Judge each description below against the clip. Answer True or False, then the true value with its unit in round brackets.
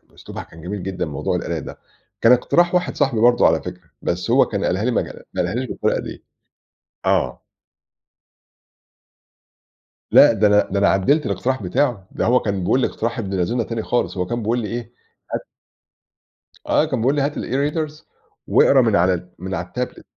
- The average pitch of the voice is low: True (115 Hz)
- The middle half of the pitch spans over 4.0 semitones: True (5.3 semitones)